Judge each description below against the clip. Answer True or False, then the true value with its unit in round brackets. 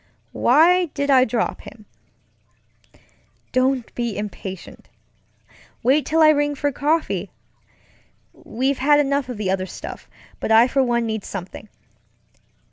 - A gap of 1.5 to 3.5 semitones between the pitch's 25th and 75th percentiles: False (4.7 semitones)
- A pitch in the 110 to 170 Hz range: False (255 Hz)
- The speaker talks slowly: True (125 wpm)